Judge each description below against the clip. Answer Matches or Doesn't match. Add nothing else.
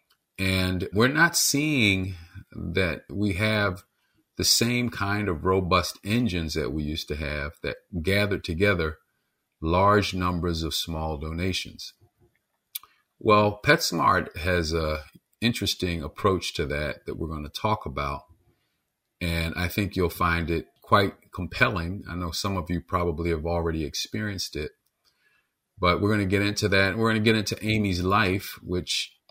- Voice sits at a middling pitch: Doesn't match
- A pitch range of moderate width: Matches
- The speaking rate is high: Doesn't match